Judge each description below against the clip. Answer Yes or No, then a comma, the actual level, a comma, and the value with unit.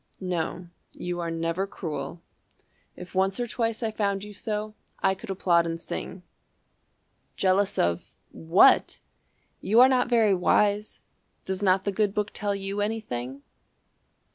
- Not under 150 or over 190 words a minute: No, average, 140 wpm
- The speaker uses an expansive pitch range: No, average, 3.0 semitones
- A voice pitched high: Yes, high, 195 Hz